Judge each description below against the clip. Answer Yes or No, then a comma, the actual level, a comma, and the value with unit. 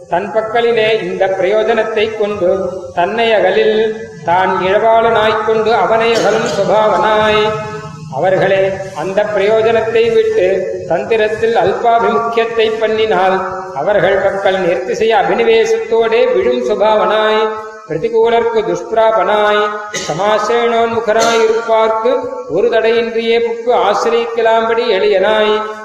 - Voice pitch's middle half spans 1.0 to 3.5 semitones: Yes, narrow, 2.4 semitones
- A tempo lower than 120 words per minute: Yes, average, 80 wpm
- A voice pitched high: Yes, high, 220 Hz